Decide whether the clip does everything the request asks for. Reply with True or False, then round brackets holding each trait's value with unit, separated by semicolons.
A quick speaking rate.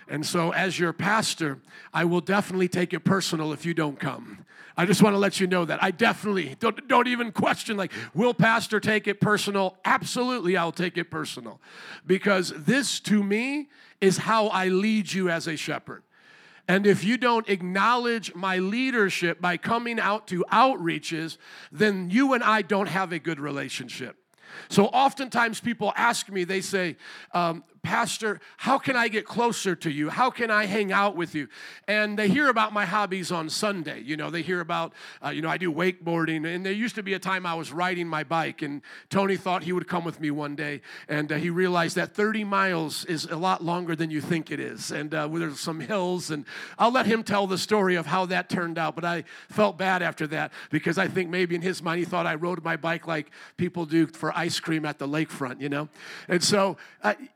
True (215 wpm)